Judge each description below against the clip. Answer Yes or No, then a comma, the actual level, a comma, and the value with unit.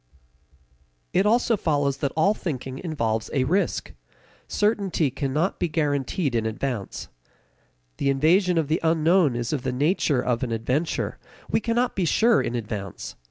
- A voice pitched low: No, medium, 150 Hz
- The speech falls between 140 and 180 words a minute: Yes, average, 150 wpm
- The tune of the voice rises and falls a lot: Yes, wide, 5.9 semitones